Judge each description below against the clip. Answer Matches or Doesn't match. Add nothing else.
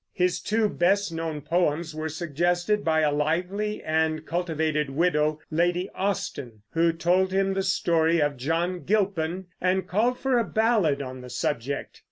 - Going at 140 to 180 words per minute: Matches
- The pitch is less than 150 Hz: Doesn't match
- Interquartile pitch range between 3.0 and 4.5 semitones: Matches